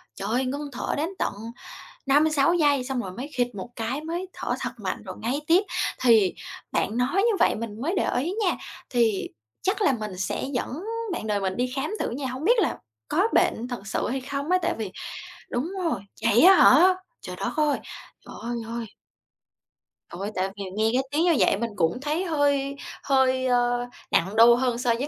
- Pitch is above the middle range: Yes, very high, 255 Hz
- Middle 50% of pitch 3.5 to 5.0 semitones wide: Yes, average, 4.6 semitones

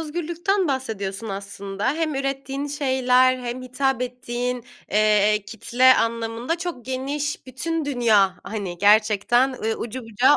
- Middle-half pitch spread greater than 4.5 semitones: No, average, 3.9 semitones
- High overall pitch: Yes, very high, 250 Hz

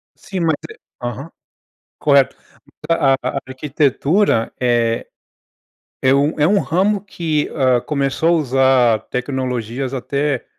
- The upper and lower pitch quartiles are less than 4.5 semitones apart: Yes, average, 3.7 semitones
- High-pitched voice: No, medium, 140 Hz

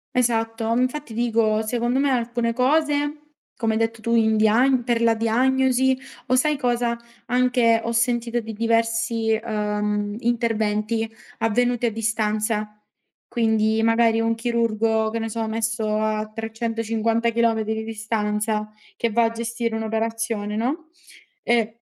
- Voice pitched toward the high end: Yes, high, 225 Hz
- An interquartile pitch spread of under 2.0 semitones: Yes, narrow, 1.4 semitones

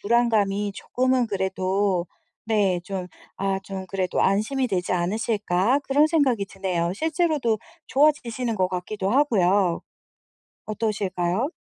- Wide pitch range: No, average, 4.4 semitones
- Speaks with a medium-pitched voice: No, high, 205 Hz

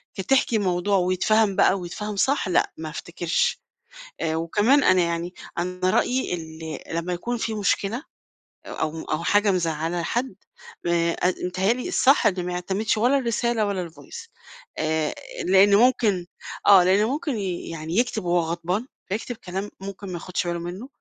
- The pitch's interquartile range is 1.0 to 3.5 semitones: No, average, 4.0 semitones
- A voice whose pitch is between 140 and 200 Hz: Yes, medium, 185 Hz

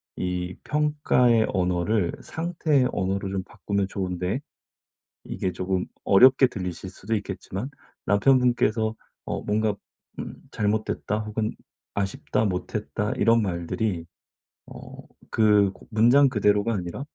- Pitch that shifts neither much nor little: Yes, average, 3.6 semitones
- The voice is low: Yes, low, 105 Hz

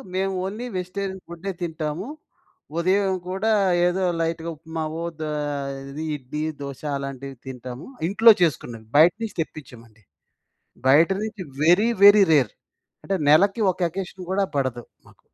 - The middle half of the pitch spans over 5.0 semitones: Yes, wide, 5.6 semitones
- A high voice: No, medium, 165 Hz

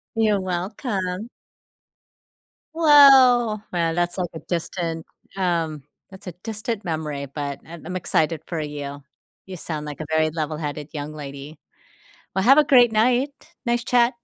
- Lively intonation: Yes, wide, 6.3 semitones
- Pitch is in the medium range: Yes, medium, 175 Hz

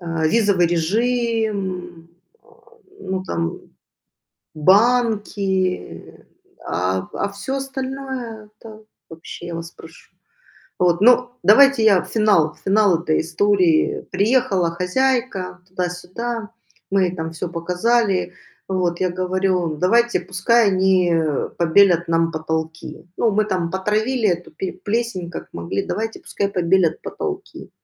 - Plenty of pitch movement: No, average, 4.4 semitones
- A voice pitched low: No, high, 190 Hz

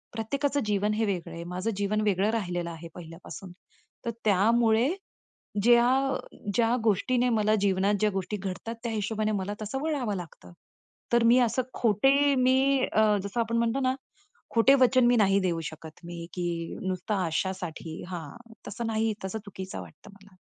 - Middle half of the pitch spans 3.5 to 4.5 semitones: Yes, average, 4.1 semitones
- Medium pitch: No, high, 210 Hz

